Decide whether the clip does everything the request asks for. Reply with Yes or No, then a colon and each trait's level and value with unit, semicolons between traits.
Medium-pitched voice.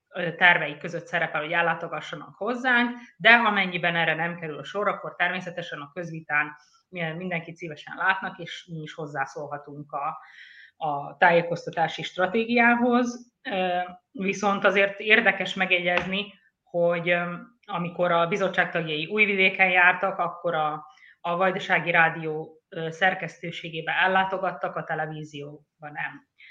Yes: medium, 175 Hz